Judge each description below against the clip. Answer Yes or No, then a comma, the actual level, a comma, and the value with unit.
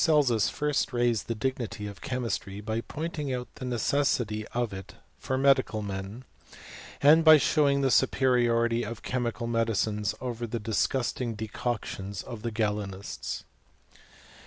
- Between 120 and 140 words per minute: Yes, slow, 135 wpm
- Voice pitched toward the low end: Yes, low, 120 Hz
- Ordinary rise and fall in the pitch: Yes, average, 3.6 semitones